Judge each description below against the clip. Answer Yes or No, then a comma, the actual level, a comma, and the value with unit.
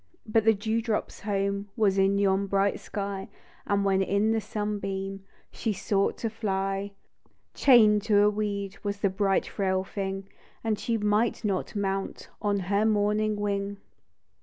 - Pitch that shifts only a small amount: Yes, narrow, 1.4 semitones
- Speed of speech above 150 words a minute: Yes, average, 160 wpm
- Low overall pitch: No, high, 200 Hz